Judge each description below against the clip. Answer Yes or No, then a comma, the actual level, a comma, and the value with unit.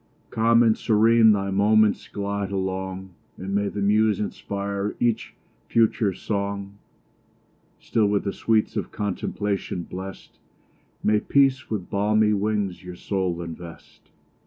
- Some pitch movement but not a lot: No, narrow, 1.9 semitones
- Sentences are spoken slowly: Yes, slow, 125 wpm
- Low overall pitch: Yes, low, 100 Hz